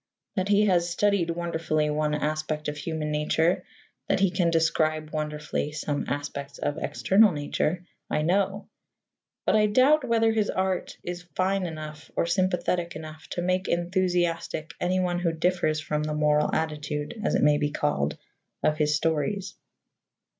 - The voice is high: No, medium, 165 Hz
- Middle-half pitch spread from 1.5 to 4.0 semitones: Yes, average, 3.3 semitones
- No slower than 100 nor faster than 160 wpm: Yes, average, 155 wpm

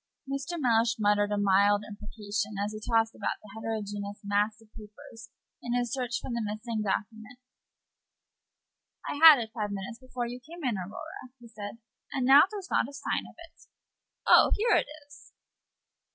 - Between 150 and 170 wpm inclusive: No, average, 180 wpm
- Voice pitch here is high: Yes, high, 225 Hz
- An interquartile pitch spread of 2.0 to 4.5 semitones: Yes, average, 3.5 semitones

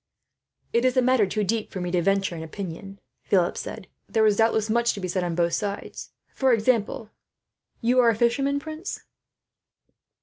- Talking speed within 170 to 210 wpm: Yes, average, 180 wpm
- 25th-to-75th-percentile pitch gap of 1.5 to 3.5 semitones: No, average, 4.0 semitones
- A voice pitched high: Yes, high, 215 Hz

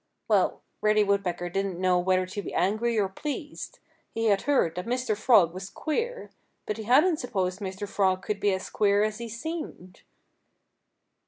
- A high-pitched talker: Yes, high, 205 Hz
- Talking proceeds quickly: No, average, 170 wpm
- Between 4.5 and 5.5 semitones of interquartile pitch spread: No, average, 3.9 semitones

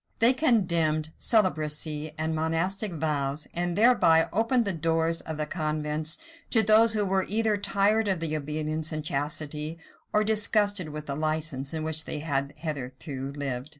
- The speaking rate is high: No, average, 155 wpm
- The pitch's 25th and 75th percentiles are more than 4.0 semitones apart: Yes, average, 4.7 semitones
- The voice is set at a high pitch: No, medium, 160 Hz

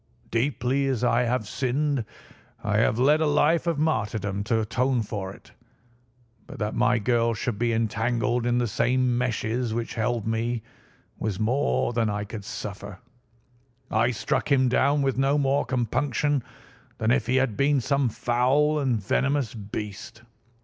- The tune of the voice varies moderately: Yes, average, 3.4 semitones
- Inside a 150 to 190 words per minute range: Yes, average, 155 wpm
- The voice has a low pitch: Yes, low, 120 Hz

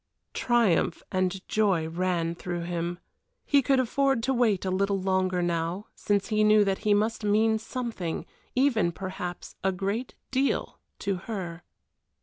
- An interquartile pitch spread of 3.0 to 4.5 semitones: Yes, average, 4.0 semitones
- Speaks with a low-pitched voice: No, high, 195 Hz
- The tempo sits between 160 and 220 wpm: No, average, 145 wpm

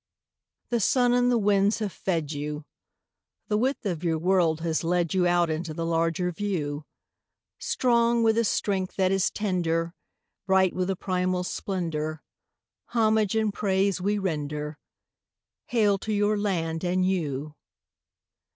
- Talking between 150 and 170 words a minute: No, average, 140 wpm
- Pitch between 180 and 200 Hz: Yes, medium, 185 Hz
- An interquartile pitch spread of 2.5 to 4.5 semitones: Yes, average, 4.0 semitones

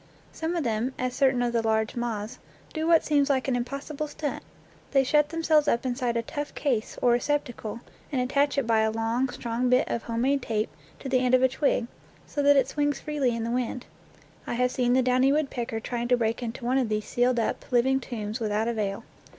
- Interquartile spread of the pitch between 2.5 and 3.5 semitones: Yes, average, 3.0 semitones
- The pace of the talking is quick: Yes, fast, 220 wpm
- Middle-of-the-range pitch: No, very high, 250 Hz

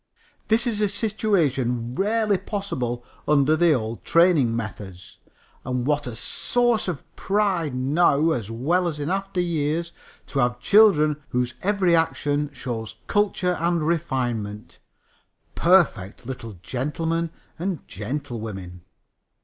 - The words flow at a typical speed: No, slow, 120 wpm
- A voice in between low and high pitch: Yes, medium, 150 Hz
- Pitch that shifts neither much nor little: No, wide, 6.7 semitones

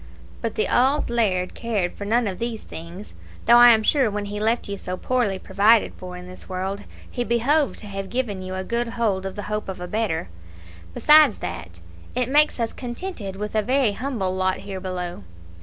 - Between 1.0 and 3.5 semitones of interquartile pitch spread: No, average, 4.1 semitones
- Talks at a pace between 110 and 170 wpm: No, fast, 205 wpm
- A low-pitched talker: No, high, 210 Hz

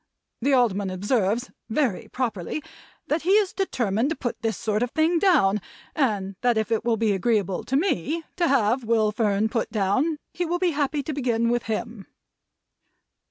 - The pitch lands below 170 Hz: No, high, 235 Hz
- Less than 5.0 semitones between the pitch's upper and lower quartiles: No, wide, 5.6 semitones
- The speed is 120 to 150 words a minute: No, average, 175 wpm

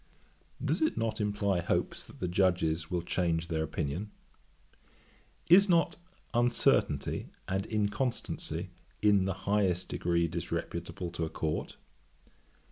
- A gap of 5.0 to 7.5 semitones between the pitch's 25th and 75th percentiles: No, average, 3.7 semitones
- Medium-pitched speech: No, very low, 95 Hz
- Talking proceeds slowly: Yes, slow, 120 wpm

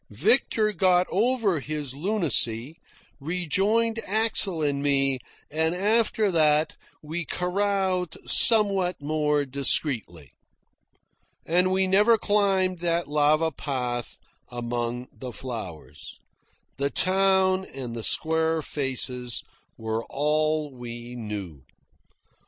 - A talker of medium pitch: Yes, medium, 155 Hz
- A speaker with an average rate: No, slow, 100 wpm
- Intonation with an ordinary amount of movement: No, wide, 6.5 semitones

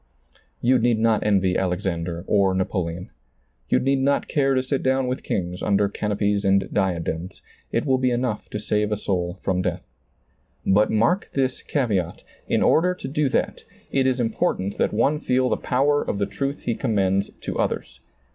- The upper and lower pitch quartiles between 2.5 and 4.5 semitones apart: No, average, 5.3 semitones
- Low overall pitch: Yes, low, 105 Hz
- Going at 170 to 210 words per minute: Yes, average, 185 wpm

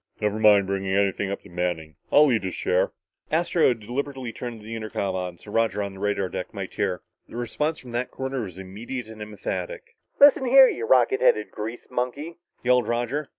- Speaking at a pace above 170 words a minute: Yes, average, 195 wpm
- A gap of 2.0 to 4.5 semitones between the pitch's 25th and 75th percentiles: No, wide, 5.4 semitones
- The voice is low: Yes, low, 115 Hz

